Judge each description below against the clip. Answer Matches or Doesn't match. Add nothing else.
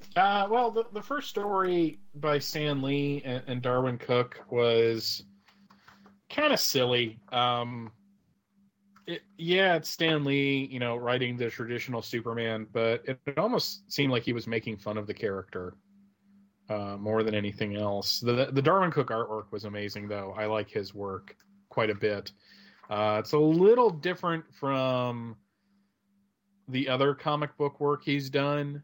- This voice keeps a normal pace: Matches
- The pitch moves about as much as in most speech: Doesn't match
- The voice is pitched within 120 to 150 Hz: Matches